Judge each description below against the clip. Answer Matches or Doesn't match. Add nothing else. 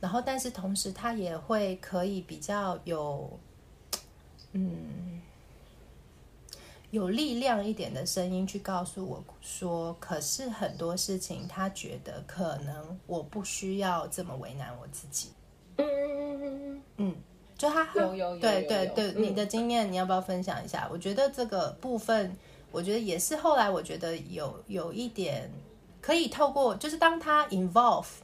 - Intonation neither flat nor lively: Matches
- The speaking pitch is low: Doesn't match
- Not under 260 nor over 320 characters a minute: Doesn't match